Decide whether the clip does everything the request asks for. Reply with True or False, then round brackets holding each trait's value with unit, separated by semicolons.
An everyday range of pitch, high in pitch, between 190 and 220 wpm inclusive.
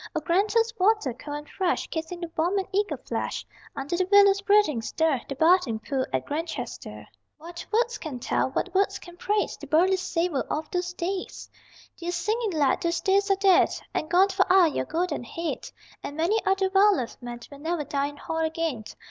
True (4.2 semitones; 345 Hz; 195 wpm)